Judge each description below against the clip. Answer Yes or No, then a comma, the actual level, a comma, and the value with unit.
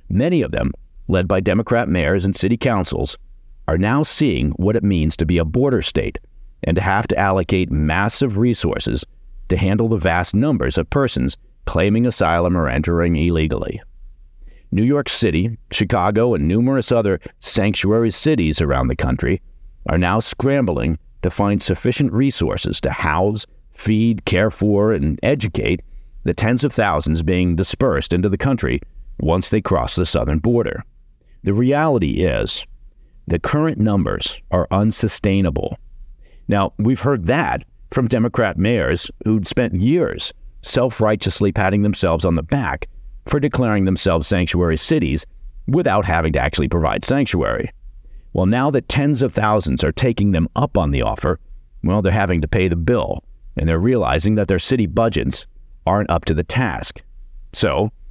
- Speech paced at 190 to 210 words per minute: No, average, 155 wpm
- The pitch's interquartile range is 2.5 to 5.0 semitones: No, wide, 5.5 semitones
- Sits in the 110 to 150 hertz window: No, very low, 95 Hz